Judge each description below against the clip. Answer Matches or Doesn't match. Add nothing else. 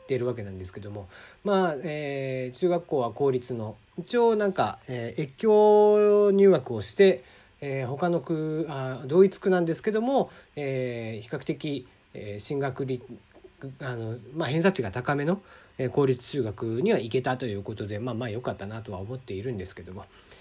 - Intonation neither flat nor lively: Doesn't match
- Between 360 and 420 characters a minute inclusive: Doesn't match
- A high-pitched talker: Doesn't match